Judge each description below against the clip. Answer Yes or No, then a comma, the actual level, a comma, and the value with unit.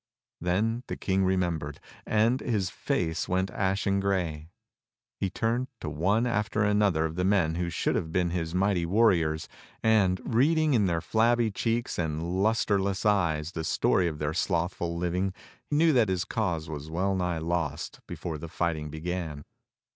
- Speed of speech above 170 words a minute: No, average, 160 wpm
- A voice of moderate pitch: No, very low, 90 Hz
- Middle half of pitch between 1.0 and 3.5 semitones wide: No, average, 4.0 semitones